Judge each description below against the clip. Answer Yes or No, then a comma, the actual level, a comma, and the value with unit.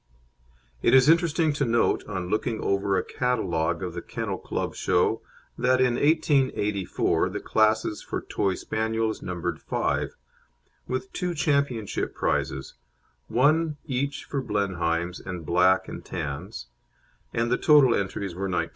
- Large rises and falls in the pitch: Yes, wide, 6.5 semitones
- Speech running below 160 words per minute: Yes, average, 140 wpm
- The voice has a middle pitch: No, low, 110 Hz